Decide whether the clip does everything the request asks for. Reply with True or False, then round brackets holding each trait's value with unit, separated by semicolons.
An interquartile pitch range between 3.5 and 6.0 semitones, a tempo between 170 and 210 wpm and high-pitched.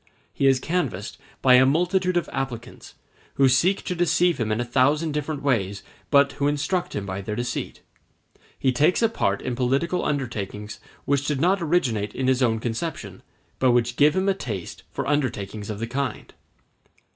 False (5.1 semitones; 180 wpm; 135 Hz)